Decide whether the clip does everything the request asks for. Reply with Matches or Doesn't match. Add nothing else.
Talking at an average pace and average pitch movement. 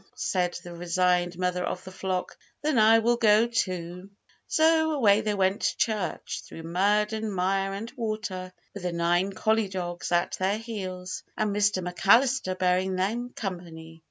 Matches